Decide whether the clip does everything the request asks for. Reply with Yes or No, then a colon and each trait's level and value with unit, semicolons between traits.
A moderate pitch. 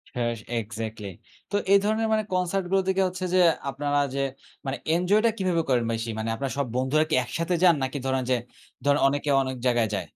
Yes: medium, 145 Hz